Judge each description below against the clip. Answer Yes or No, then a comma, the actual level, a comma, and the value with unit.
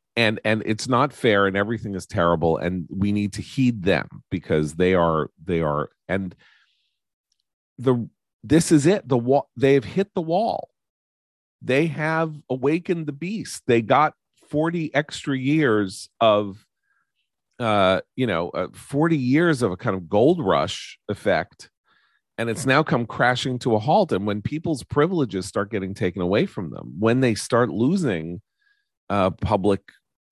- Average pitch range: No, wide, 7.2 semitones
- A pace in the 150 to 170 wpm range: Yes, average, 155 wpm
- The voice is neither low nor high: No, low, 115 Hz